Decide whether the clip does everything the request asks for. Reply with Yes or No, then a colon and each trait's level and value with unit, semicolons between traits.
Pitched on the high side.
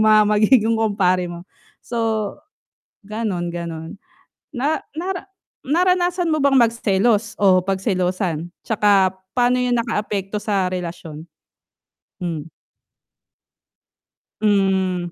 Yes: high, 205 Hz